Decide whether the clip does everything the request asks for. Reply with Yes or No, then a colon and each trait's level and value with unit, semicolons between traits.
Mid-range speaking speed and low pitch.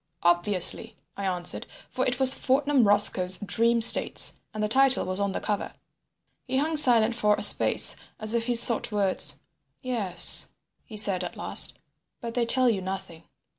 No: average, 170 wpm; high, 215 Hz